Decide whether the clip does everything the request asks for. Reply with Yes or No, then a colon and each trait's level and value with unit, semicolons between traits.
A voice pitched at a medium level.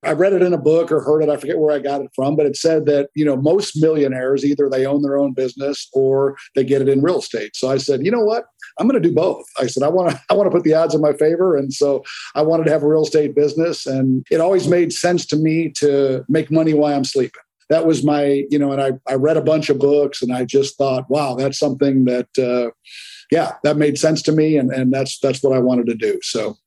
Yes: medium, 145 Hz